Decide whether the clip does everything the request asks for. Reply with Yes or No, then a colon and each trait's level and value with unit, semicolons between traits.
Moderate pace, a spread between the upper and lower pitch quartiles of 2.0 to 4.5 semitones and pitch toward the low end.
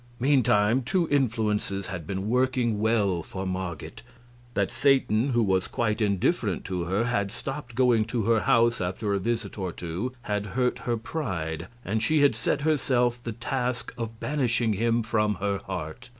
Yes: average, 165 wpm; average, 3.9 semitones; low, 110 Hz